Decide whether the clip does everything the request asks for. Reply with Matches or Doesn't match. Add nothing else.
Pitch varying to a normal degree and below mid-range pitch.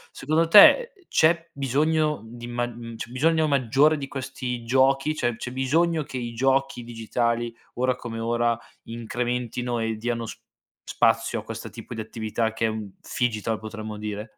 Matches